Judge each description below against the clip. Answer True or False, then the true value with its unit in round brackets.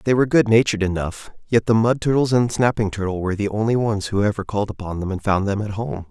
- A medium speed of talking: False (245 wpm)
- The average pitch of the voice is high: False (105 Hz)